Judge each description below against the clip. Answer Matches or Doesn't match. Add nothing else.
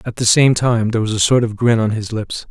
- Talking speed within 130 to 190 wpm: Doesn't match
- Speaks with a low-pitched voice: Matches